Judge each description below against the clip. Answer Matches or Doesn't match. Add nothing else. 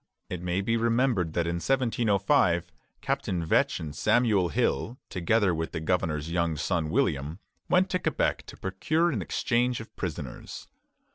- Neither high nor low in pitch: Doesn't match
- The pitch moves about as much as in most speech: Doesn't match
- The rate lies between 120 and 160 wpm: Matches